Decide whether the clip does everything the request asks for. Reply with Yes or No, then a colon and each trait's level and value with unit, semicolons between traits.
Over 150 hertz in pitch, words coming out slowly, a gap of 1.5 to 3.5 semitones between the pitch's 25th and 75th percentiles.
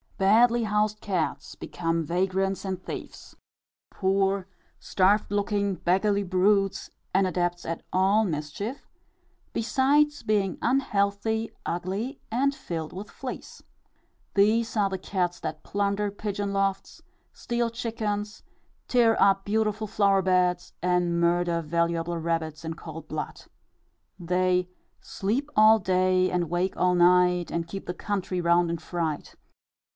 Yes: high, 190 Hz; slow, 125 wpm; average, 3.1 semitones